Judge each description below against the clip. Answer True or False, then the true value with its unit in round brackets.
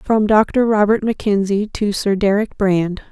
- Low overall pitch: False (205 Hz)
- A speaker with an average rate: True (155 wpm)